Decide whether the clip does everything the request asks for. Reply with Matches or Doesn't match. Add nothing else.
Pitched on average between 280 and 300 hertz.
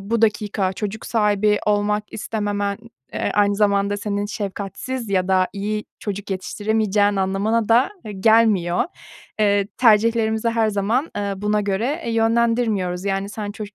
Doesn't match